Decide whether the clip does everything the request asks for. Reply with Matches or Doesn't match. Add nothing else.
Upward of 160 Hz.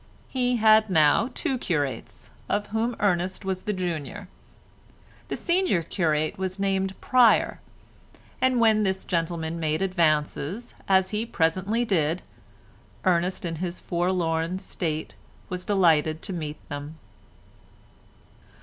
Matches